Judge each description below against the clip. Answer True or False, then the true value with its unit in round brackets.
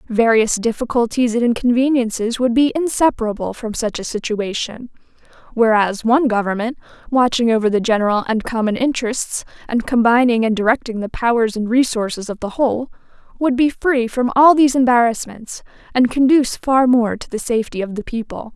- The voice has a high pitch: True (235 Hz)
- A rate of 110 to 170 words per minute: True (160 wpm)